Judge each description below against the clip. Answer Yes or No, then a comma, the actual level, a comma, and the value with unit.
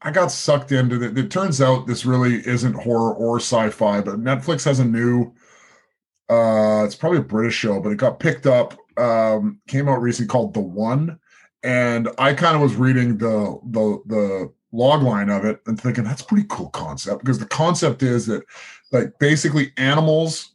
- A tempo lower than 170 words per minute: No, average, 190 wpm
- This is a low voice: Yes, low, 125 Hz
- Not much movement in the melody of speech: No, average, 4.0 semitones